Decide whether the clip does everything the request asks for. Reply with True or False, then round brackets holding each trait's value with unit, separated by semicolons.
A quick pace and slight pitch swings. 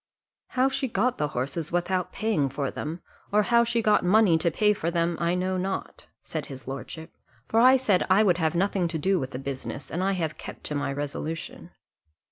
False (210 wpm; 5.3 semitones)